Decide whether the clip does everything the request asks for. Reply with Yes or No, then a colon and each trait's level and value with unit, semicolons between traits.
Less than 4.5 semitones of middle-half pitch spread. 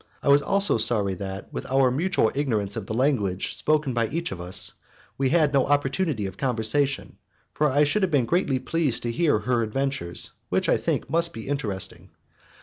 No: average, 5.0 semitones